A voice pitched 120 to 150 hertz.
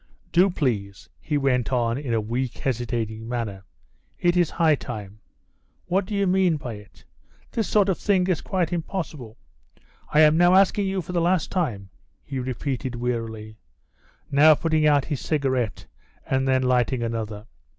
Yes: low, 135 Hz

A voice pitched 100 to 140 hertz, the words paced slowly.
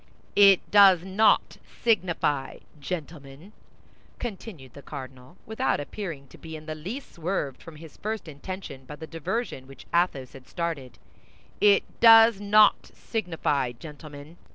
No: medium, 165 Hz; slow, 130 wpm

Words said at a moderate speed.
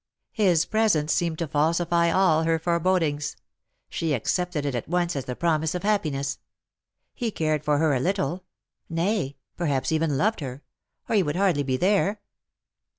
Yes: average, 170 wpm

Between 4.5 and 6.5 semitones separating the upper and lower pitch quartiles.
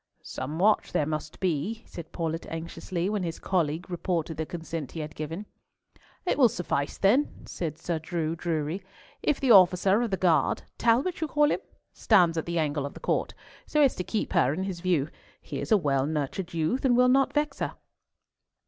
Yes: average, 4.8 semitones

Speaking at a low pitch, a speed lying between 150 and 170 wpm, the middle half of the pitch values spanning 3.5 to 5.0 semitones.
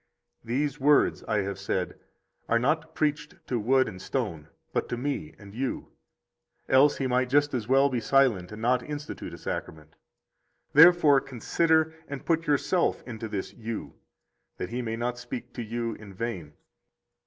Yes: low, 125 Hz; average, 165 wpm; average, 4.4 semitones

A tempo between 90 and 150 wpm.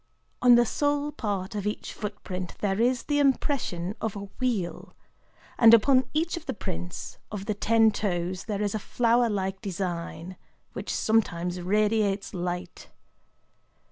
Yes: average, 145 wpm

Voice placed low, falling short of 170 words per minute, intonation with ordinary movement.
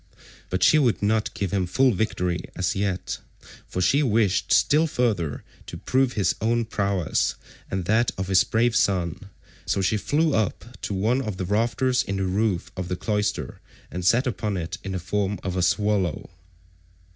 No: low, 100 Hz; average, 180 wpm; average, 3.7 semitones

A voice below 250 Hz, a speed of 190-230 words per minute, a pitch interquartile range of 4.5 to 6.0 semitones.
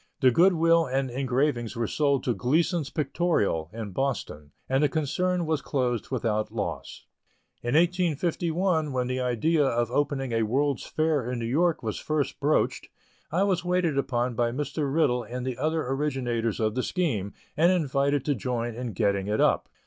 No: low, 135 Hz; average, 175 wpm; average, 4.8 semitones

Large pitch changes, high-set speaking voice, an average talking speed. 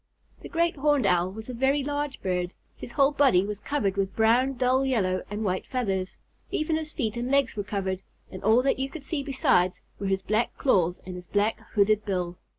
No: wide, 6.1 semitones; high, 220 Hz; fast, 210 wpm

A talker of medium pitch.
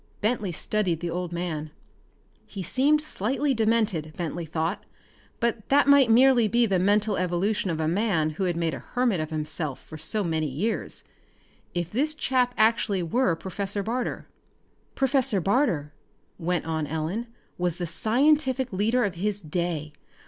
No: high, 195 Hz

